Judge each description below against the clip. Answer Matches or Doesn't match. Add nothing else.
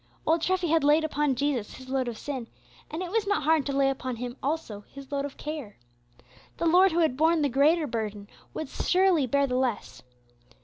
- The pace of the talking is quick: Matches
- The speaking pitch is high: Matches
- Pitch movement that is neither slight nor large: Matches